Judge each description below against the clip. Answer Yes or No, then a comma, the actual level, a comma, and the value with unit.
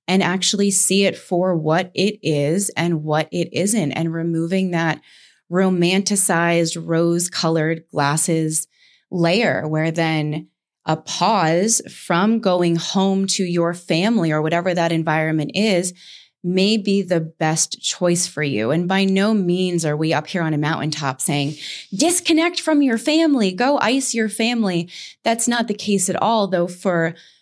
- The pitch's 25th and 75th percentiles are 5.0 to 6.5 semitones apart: No, average, 3.5 semitones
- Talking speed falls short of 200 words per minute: Yes, average, 150 wpm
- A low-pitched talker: No, medium, 175 Hz